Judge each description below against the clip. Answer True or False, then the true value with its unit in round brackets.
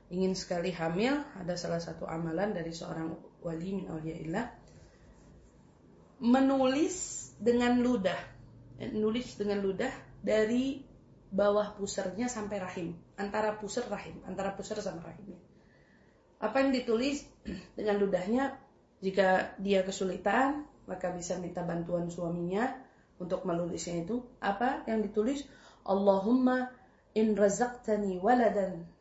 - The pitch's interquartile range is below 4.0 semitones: False (5.3 semitones)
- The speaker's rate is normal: True (110 wpm)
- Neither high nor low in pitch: False (200 Hz)